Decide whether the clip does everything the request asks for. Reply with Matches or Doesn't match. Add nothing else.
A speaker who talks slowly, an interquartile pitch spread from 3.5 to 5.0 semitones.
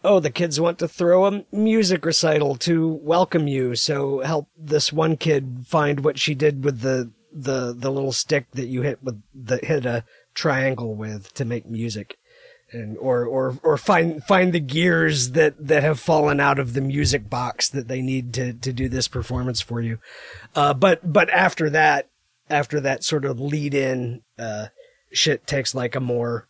Doesn't match